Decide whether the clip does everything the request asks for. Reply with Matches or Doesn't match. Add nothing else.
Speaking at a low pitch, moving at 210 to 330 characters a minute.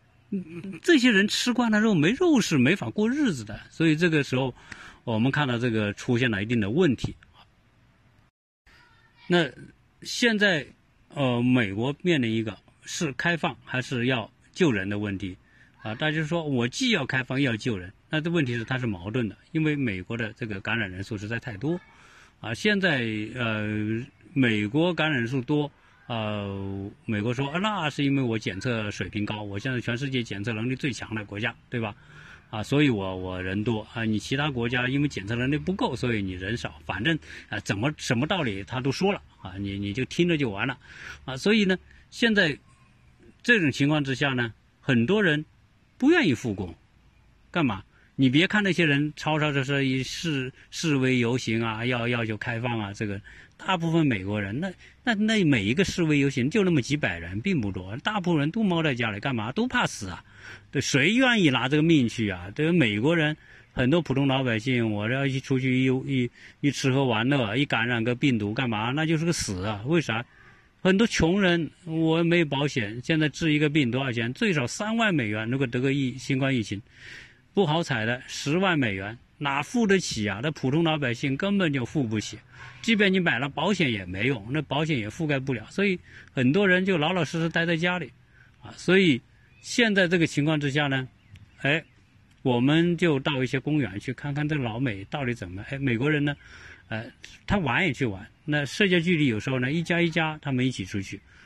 Matches